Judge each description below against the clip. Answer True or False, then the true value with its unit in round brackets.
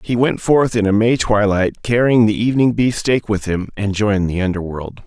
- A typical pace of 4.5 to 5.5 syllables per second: True (5.2 syllables/s)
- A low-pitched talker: True (110 Hz)